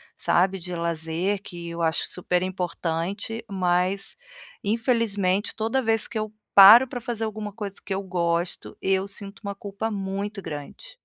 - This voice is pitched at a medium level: No, high, 195 Hz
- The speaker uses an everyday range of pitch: Yes, average, 3.3 semitones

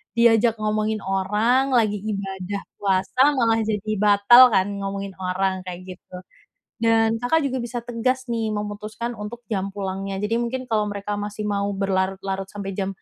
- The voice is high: Yes, high, 210 Hz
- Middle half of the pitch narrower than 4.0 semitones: Yes, average, 2.7 semitones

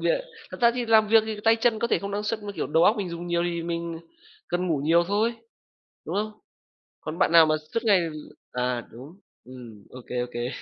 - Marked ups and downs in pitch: Yes, wide, 5.7 semitones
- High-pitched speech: No, medium, 175 Hz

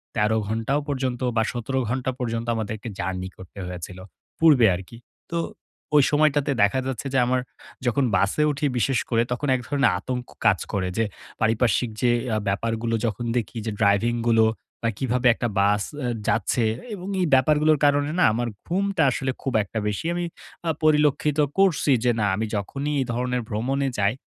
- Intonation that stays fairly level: No, average, 4.2 semitones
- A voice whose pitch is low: Yes, low, 120 Hz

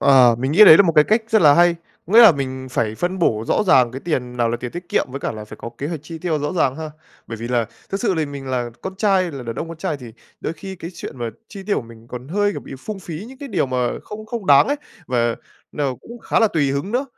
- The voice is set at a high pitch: No, medium, 150 Hz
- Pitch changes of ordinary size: No, wide, 7.1 semitones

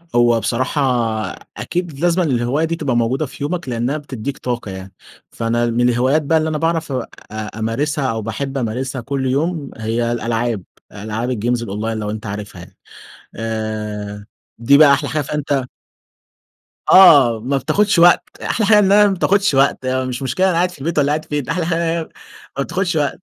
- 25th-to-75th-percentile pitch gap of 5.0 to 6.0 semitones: Yes, average, 5.3 semitones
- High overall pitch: No, low, 135 Hz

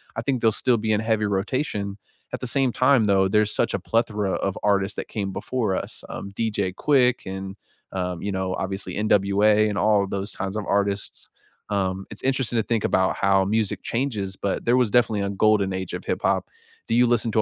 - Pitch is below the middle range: Yes, low, 105 Hz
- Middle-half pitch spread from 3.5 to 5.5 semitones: No, average, 2.7 semitones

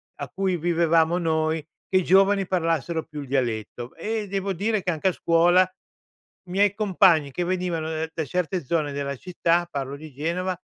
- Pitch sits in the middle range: Yes, medium, 170 Hz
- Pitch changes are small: No, average, 3.0 semitones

